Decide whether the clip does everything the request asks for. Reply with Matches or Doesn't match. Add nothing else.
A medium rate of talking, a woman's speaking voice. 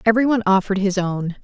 Matches